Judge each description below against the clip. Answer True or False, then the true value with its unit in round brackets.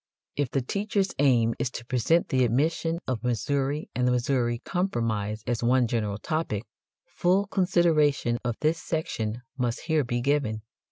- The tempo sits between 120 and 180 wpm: True (155 wpm)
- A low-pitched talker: True (130 Hz)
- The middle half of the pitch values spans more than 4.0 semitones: True (5.1 semitones)